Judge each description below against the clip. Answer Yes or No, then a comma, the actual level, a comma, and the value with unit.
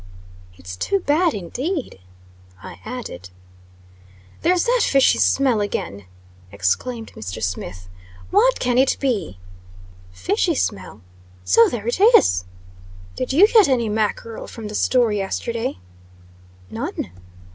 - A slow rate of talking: Yes, slow, 115 wpm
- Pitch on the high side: Yes, high, 225 Hz